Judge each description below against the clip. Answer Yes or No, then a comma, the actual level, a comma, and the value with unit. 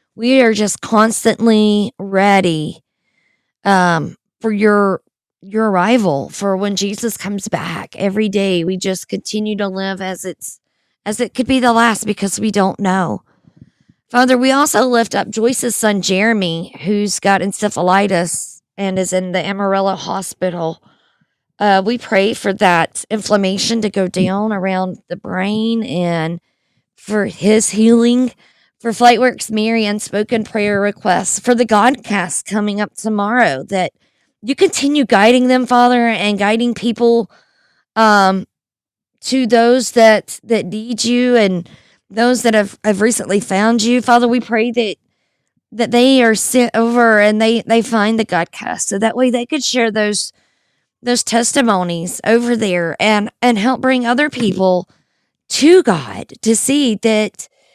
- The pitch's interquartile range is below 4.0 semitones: Yes, average, 3.4 semitones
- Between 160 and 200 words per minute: No, average, 145 wpm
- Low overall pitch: No, high, 215 Hz